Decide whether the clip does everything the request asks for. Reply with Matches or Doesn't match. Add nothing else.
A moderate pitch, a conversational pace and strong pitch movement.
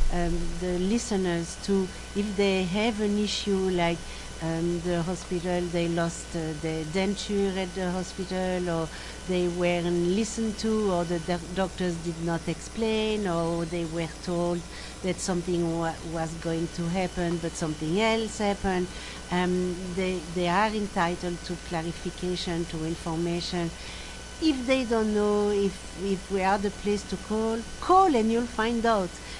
Doesn't match